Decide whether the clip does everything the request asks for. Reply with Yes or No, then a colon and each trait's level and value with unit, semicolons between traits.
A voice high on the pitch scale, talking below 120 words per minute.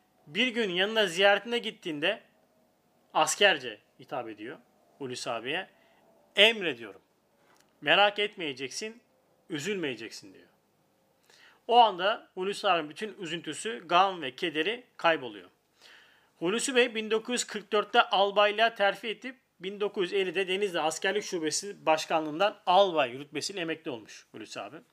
Yes: high, 205 Hz; average, 100 wpm